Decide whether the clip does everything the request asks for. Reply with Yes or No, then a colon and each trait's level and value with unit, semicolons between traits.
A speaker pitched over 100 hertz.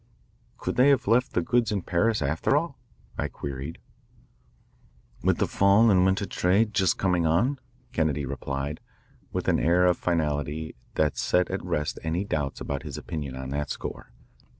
No: very low, 85 Hz